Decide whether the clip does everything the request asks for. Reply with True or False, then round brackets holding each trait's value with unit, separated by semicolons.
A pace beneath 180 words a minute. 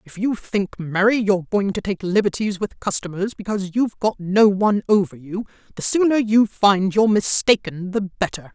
False (185 wpm)